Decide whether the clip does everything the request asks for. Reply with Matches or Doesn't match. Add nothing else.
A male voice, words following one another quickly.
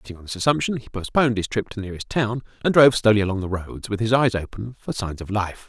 Matches